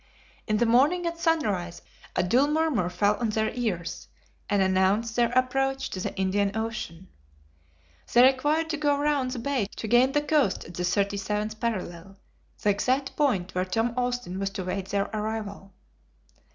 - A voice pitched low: No, high, 220 Hz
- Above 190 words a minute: No, average, 165 wpm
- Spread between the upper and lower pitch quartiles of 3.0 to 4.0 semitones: No, average, 5.3 semitones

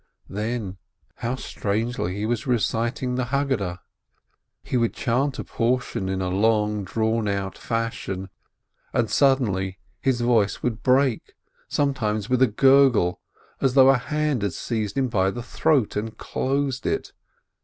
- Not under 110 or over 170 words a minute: Yes, average, 145 wpm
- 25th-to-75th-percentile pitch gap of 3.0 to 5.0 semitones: Yes, average, 4.0 semitones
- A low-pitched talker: Yes, low, 115 Hz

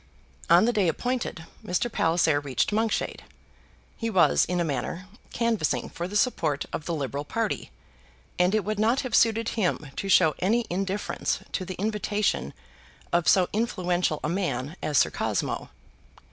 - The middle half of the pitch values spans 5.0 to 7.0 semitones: Yes, average, 5.3 semitones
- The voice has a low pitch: No, medium, 185 Hz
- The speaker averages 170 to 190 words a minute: No, average, 160 wpm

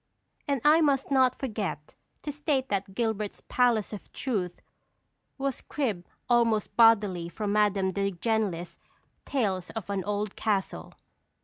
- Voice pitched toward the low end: No, high, 215 Hz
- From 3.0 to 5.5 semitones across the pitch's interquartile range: Yes, average, 4.4 semitones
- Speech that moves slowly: Yes, slow, 130 wpm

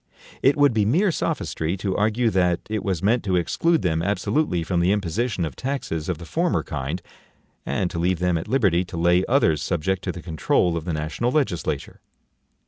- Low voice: Yes, very low, 90 Hz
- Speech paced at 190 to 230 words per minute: Yes, average, 195 wpm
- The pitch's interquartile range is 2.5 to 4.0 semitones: No, wide, 5.4 semitones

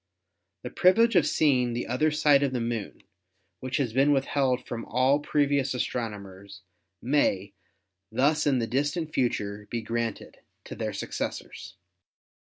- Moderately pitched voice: No, low, 130 Hz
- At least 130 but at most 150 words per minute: Yes, average, 140 wpm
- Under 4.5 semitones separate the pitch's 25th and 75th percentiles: Yes, average, 4.0 semitones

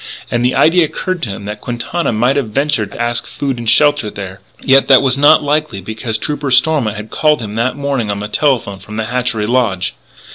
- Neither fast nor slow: No, fast, 215 wpm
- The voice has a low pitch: Yes, low, 120 Hz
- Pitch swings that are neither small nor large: Yes, average, 4.8 semitones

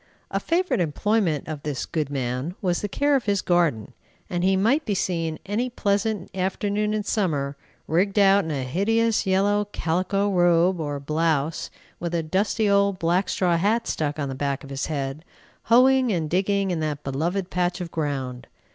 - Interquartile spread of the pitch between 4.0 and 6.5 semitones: Yes, average, 4.8 semitones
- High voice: No, medium, 180 Hz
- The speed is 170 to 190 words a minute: Yes, average, 180 wpm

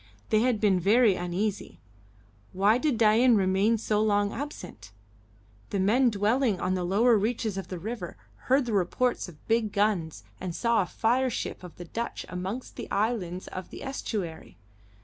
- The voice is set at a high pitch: Yes, high, 210 Hz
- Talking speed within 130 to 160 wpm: No, average, 170 wpm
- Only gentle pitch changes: No, average, 4.1 semitones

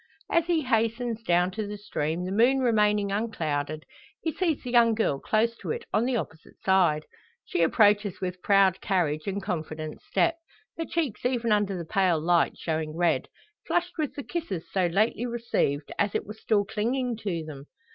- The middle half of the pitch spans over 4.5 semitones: Yes, wide, 5.4 semitones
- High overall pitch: Yes, high, 205 Hz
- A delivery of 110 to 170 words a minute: No, average, 180 wpm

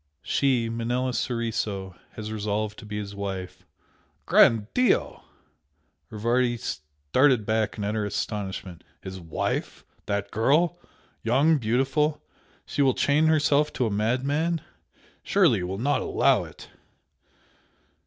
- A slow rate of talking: Yes, slow, 120 wpm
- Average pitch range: Yes, average, 5.0 semitones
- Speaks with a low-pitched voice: Yes, low, 115 Hz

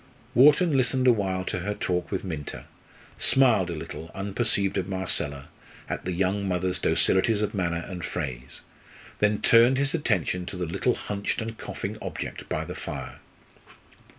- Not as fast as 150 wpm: No, average, 160 wpm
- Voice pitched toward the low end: Yes, very low, 95 Hz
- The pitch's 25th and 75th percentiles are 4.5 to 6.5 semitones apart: No, average, 4.0 semitones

